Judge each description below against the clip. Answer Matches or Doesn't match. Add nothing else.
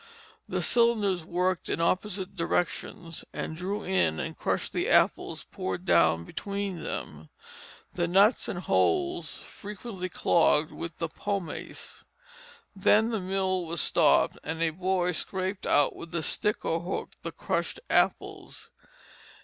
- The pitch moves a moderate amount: Matches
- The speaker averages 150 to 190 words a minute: Doesn't match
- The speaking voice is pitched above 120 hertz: Matches